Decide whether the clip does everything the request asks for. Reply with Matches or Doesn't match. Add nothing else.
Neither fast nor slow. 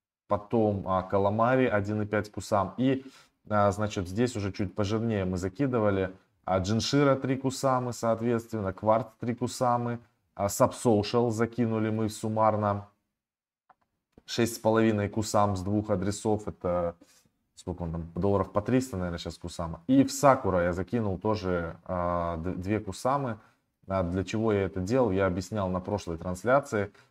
Matches